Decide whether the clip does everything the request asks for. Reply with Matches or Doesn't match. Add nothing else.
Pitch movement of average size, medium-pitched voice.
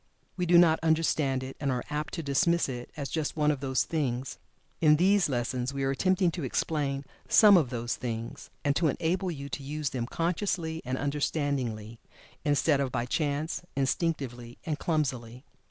Matches